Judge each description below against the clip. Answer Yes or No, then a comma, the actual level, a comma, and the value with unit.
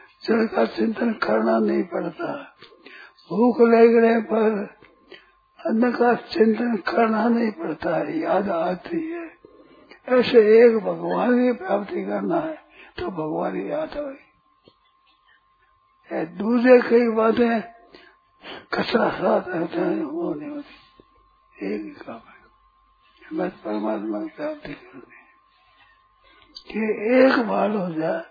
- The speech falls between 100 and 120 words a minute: Yes, slow, 110 wpm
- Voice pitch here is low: No, high, 245 Hz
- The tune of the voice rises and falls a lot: Yes, wide, 7.2 semitones